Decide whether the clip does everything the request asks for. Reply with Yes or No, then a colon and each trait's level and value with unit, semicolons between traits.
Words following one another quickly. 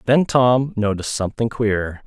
No: average, 145 wpm